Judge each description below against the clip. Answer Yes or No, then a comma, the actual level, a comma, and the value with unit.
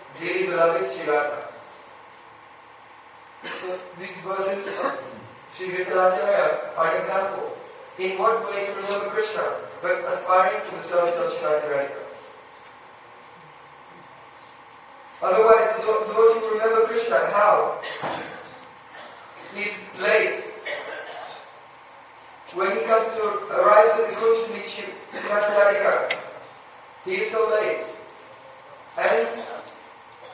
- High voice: Yes, high, 210 Hz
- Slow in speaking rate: Yes, slow, 100 wpm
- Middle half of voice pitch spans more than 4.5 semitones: No, average, 3.6 semitones